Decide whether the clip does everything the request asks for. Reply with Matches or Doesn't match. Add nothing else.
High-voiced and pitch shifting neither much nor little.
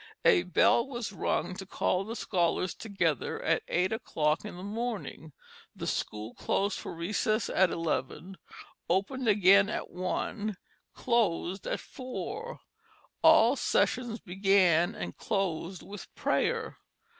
Matches